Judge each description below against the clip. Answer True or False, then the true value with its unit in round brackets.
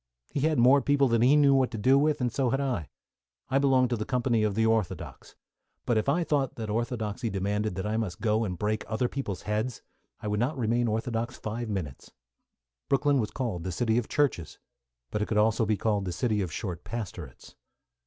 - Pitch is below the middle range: True (115 Hz)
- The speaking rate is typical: False (215 wpm)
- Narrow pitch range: False (3.5 semitones)